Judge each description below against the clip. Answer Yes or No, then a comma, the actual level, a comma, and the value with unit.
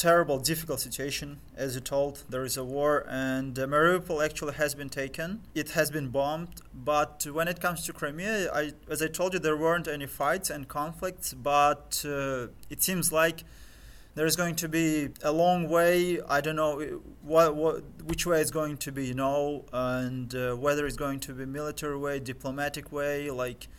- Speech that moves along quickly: No, average, 190 wpm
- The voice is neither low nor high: Yes, medium, 150 Hz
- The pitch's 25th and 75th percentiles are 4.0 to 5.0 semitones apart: No, average, 2.9 semitones